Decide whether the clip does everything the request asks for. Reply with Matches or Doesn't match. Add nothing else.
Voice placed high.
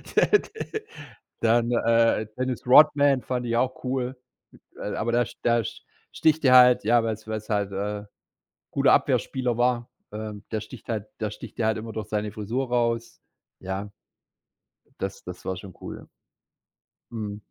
Doesn't match